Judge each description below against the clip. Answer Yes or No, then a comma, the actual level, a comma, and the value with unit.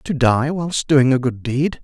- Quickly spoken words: Yes, fast, 230 wpm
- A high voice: No, low, 135 Hz